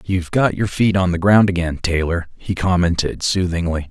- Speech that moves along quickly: No, average, 185 wpm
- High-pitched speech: No, very low, 90 Hz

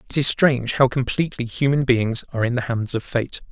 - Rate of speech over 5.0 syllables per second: Yes, 5.9 syllables/s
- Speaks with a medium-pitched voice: No, low, 125 Hz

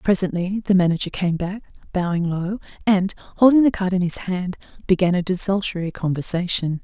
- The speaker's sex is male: No, female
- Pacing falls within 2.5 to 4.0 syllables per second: No, 5.5 syllables/s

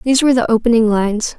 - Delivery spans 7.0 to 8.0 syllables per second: Yes, 7.6 syllables/s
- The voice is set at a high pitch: Yes, high, 230 Hz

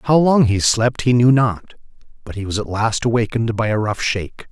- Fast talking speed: Yes, fast, 225 wpm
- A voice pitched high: No, low, 115 Hz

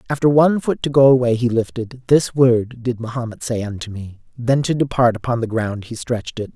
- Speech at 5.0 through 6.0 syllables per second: Yes, 5.5 syllables/s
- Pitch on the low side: Yes, low, 120 Hz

